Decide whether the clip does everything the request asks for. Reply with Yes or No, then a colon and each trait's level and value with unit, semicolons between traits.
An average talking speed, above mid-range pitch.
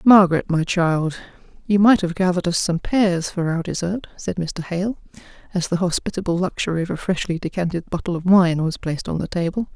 No: average, 195 wpm; medium, 180 Hz